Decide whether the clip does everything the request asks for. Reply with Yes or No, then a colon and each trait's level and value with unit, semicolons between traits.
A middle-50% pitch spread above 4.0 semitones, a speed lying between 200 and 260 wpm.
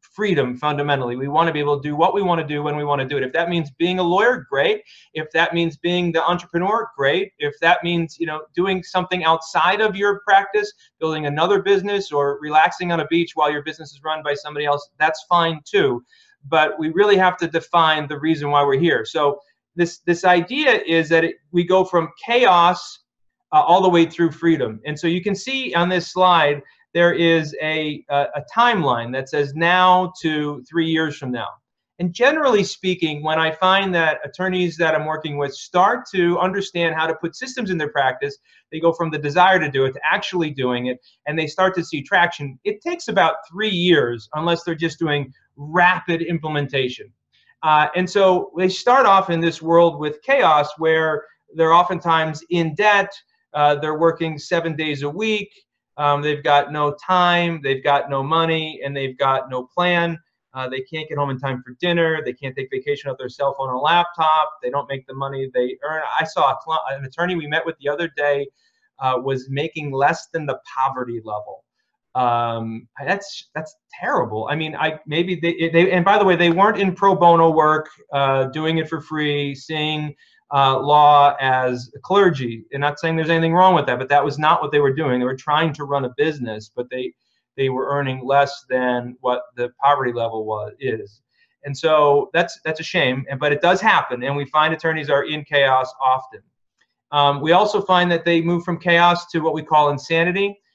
No: average, 3.5 semitones; fast, 205 wpm